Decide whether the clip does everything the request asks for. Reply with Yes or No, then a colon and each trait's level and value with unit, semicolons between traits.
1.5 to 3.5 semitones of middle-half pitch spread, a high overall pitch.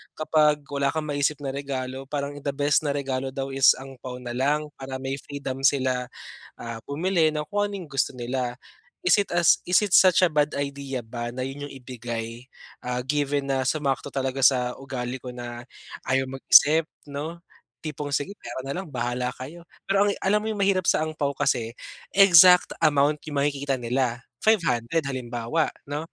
No: average, 2.9 semitones; medium, 140 Hz